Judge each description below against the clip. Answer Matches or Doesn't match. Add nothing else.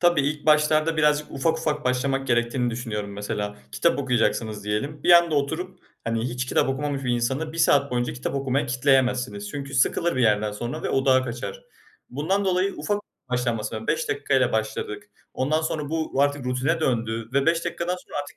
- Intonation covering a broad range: Doesn't match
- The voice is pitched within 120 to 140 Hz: Matches